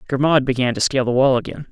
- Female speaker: No, male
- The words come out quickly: Yes, fast, 245 wpm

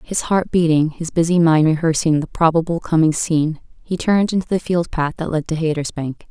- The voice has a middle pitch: Yes, medium, 165 Hz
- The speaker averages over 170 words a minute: Yes, average, 200 wpm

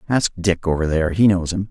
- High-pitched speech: No, very low, 90 Hz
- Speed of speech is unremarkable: No, fast, 245 wpm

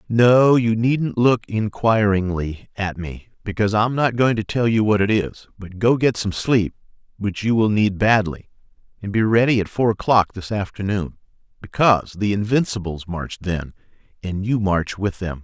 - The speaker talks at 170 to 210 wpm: Yes, average, 175 wpm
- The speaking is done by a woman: No, male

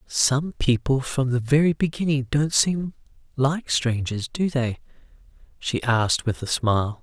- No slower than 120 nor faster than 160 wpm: Yes, average, 145 wpm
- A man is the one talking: Yes, male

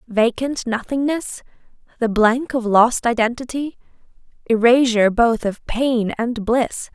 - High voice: Yes, high, 240 Hz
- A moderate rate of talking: No, slow, 110 wpm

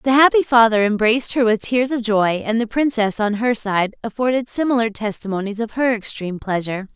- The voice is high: Yes, high, 225 Hz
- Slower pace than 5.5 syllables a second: No, 5.6 syllables/s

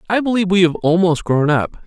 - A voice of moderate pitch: Yes, medium, 180 Hz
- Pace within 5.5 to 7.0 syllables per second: Yes, 6.1 syllables/s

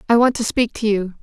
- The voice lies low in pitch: No, high, 225 Hz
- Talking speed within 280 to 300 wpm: Yes, fast, 295 wpm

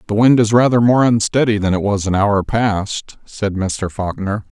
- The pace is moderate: Yes, average, 195 wpm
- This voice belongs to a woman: No, male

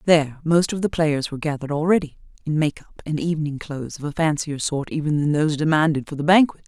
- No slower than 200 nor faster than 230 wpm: Yes, fast, 205 wpm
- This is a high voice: No, medium, 155 Hz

